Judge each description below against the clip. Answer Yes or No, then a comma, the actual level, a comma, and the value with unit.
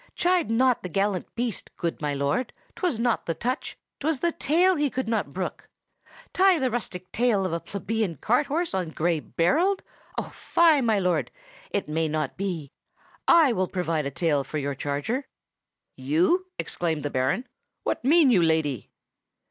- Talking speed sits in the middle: Yes, average, 170 wpm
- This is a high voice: Yes, high, 200 Hz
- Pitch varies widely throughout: Yes, wide, 8.6 semitones